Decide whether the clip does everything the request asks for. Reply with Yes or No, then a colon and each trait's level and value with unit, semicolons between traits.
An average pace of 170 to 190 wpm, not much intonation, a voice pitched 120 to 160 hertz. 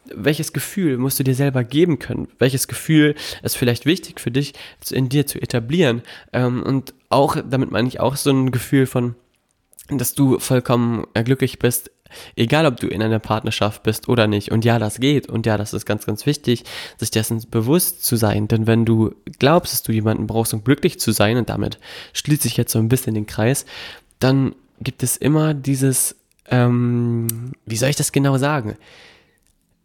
No: average, 185 wpm; average, 3.4 semitones; low, 125 Hz